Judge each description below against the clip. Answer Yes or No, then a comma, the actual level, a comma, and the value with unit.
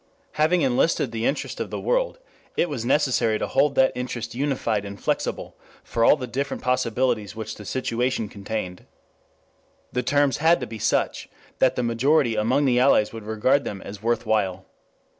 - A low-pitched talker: Yes, low, 125 Hz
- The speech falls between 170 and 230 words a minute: Yes, average, 175 wpm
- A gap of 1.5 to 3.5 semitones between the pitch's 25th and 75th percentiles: No, average, 3.9 semitones